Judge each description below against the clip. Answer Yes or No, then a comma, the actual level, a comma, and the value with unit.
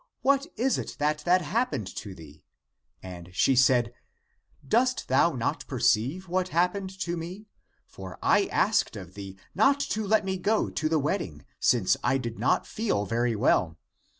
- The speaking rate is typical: Yes, average, 165 wpm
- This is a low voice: No, medium, 155 Hz